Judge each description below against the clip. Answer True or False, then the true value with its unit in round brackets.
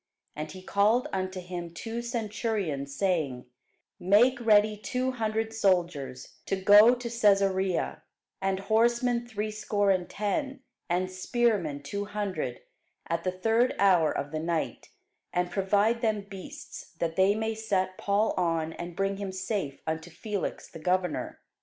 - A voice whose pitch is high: True (195 Hz)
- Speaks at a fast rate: False (140 wpm)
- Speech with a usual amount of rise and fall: True (3.8 semitones)